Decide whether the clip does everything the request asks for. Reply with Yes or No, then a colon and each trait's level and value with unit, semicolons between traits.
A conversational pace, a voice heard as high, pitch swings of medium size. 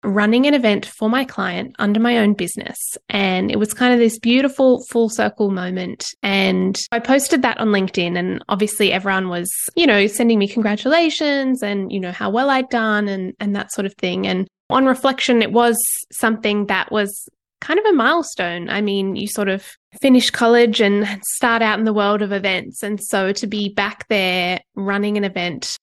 Yes: average, 195 wpm; high, 210 Hz; average, 3.4 semitones